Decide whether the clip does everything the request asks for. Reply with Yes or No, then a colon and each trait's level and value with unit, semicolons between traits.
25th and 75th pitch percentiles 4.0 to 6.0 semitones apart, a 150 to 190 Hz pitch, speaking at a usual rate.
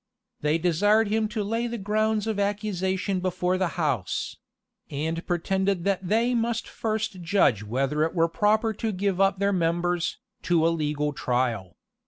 Yes: average, 4.3 semitones; medium, 185 Hz; average, 160 wpm